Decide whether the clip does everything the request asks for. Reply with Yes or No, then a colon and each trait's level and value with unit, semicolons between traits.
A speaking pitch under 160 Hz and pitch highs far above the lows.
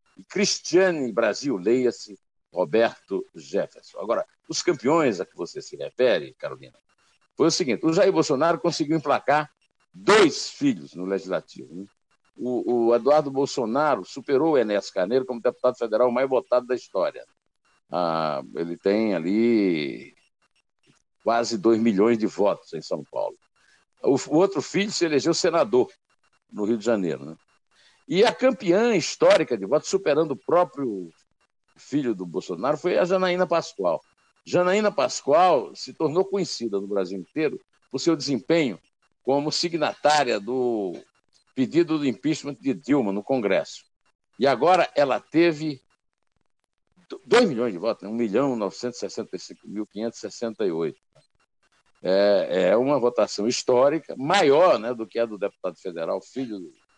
Yes: low, 135 Hz; wide, 7.5 semitones